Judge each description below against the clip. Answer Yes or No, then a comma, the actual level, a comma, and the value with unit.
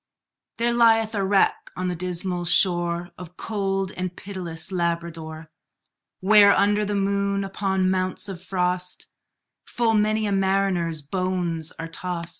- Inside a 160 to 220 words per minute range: No, slow, 135 wpm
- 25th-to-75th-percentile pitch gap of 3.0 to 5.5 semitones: No, narrow, 2.4 semitones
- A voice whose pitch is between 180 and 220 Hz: Yes, medium, 185 Hz